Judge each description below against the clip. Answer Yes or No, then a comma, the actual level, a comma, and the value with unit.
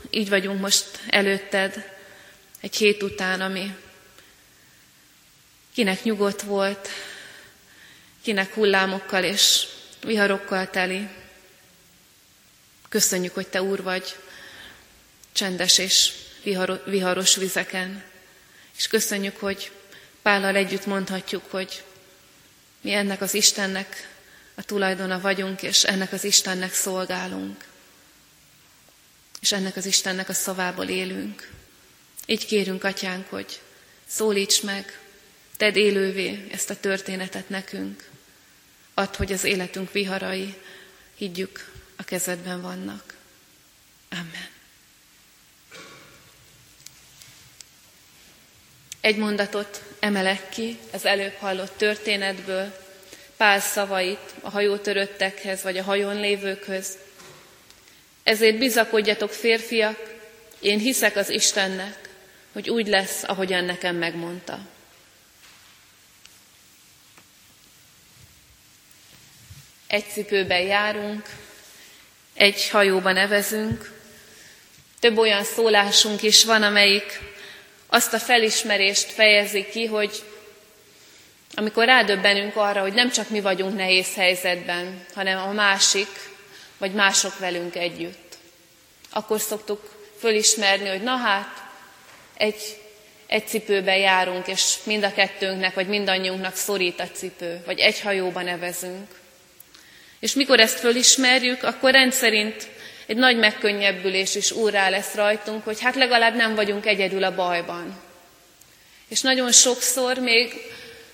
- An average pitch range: No, narrow, 2.0 semitones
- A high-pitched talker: Yes, high, 195 Hz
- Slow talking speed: Yes, slow, 100 wpm